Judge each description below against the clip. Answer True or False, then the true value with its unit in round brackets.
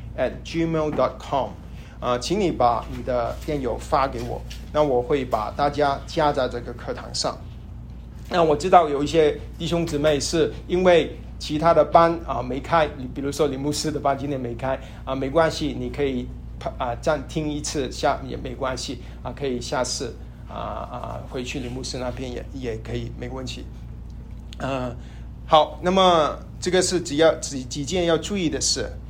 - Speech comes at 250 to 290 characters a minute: True (260 characters per minute)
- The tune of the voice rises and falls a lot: False (4.0 semitones)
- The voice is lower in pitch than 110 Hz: False (140 Hz)